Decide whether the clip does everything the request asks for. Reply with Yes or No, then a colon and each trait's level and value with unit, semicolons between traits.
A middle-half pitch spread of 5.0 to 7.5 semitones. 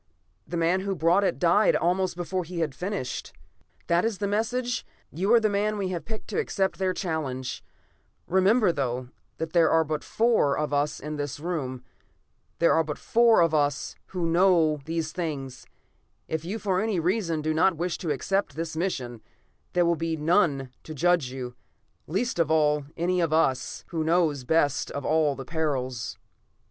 No: average, 3.9 semitones